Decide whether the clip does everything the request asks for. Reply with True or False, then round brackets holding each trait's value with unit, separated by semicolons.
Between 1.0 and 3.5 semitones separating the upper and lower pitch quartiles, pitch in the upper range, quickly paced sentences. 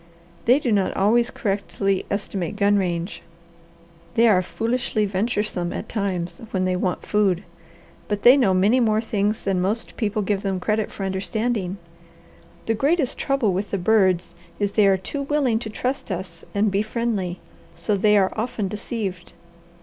False (2.9 semitones; 205 Hz; 165 wpm)